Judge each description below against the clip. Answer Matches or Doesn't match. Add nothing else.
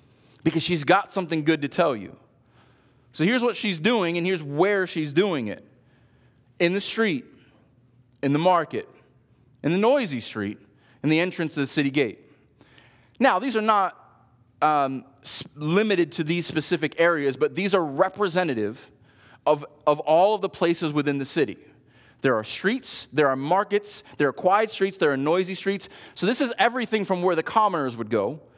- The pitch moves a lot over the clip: Matches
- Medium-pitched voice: Matches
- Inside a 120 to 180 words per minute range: Matches